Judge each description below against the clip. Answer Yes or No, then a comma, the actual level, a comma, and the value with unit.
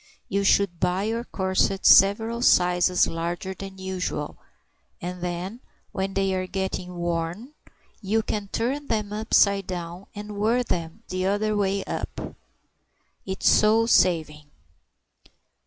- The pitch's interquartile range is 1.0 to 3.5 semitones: Yes, average, 2.7 semitones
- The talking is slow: Yes, slow, 125 wpm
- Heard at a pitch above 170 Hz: Yes, high, 190 Hz